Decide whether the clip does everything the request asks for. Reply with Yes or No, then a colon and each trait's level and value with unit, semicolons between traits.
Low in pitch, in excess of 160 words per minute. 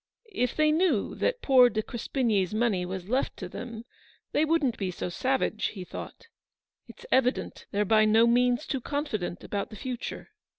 No: high, 235 Hz; average, 180 wpm